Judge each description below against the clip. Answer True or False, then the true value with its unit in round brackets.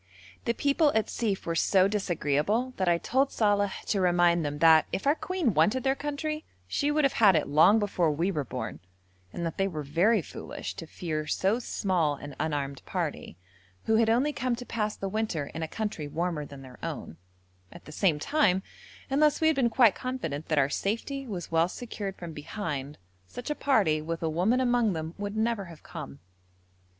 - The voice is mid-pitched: False (195 Hz)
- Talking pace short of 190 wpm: False (200 wpm)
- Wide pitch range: True (6.9 semitones)